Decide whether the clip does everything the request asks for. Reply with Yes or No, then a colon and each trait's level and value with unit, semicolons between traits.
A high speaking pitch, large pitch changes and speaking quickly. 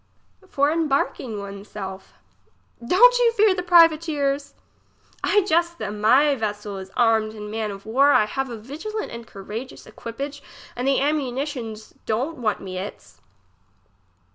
No: very high, 255 Hz; wide, 6.2 semitones; average, 145 wpm